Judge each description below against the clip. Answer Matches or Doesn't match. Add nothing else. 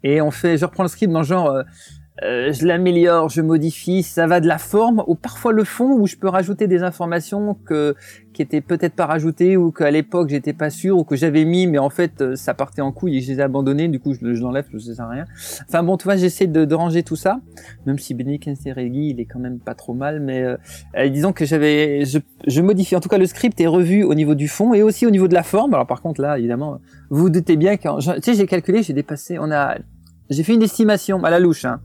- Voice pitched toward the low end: Doesn't match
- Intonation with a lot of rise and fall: Doesn't match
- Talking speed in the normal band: Doesn't match